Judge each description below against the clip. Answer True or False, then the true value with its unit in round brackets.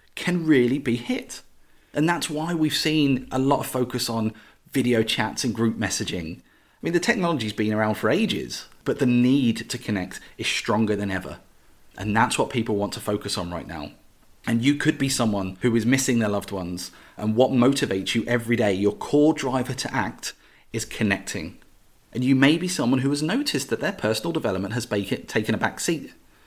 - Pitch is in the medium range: False (120 Hz)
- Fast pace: False (195 wpm)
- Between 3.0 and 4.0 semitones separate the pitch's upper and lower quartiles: False (4.8 semitones)